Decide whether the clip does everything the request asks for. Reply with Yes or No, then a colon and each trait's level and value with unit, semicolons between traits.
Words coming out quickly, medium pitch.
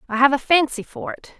No: fast, 260 wpm; very high, 275 Hz